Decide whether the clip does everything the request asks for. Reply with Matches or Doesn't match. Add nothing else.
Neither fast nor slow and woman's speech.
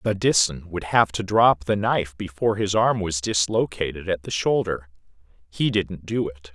Doesn't match